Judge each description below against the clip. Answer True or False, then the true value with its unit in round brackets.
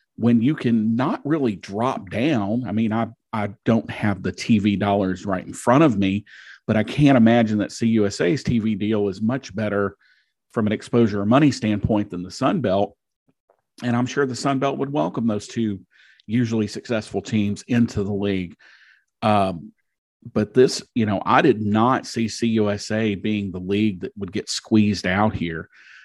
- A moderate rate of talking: True (175 wpm)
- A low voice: True (110 Hz)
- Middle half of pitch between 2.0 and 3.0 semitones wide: True (2.6 semitones)